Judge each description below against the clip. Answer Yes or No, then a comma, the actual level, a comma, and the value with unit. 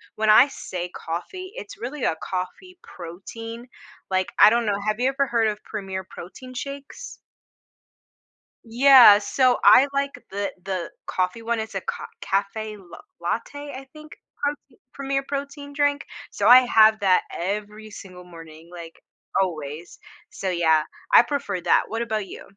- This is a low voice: No, high, 215 Hz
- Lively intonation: Yes, wide, 6.4 semitones